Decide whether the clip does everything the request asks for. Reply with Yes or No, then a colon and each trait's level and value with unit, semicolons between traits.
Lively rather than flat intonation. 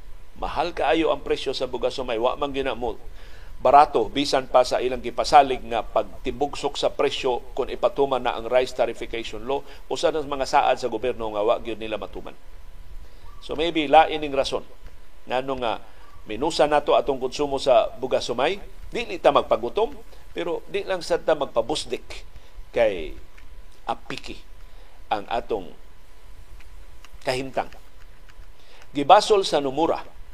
Yes: wide, 7.4 semitones